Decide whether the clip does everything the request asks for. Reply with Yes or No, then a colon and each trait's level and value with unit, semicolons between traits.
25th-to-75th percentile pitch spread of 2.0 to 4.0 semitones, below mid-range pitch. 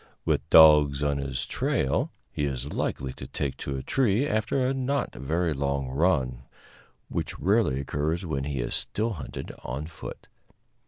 No: wide, 5.6 semitones; very low, 75 Hz